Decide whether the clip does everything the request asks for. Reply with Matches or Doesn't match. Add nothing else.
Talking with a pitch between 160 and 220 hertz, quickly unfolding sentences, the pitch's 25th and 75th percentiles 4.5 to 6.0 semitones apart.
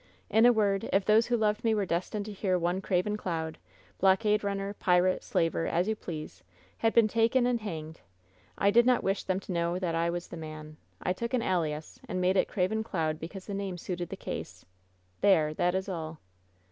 Doesn't match